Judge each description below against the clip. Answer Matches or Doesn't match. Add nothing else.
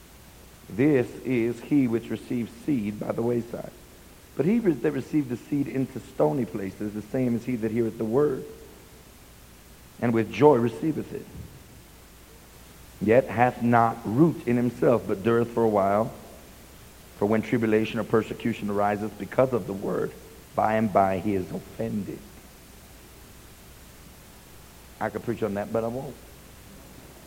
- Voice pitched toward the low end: Matches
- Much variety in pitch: Doesn't match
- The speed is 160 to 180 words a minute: Doesn't match